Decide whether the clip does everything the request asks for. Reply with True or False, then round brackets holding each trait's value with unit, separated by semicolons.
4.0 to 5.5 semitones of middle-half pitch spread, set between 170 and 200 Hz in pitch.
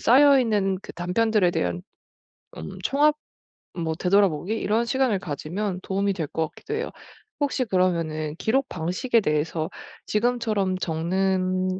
True (5.2 semitones; 190 Hz)